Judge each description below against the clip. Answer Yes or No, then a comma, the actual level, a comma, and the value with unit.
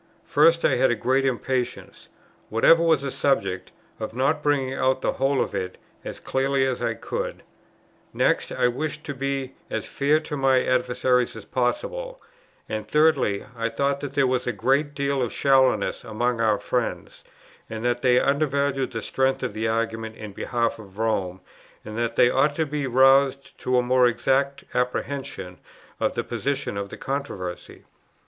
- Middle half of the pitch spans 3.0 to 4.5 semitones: Yes, average, 3.3 semitones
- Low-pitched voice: Yes, low, 130 Hz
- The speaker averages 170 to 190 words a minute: Yes, average, 175 wpm